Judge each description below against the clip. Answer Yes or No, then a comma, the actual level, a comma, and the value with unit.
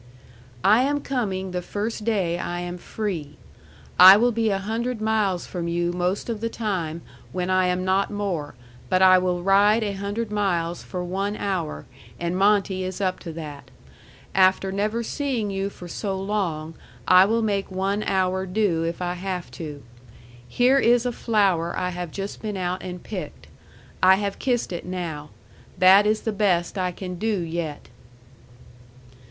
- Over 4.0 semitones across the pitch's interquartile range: No, average, 2.9 semitones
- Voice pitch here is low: No, high, 190 Hz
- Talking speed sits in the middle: Yes, average, 170 wpm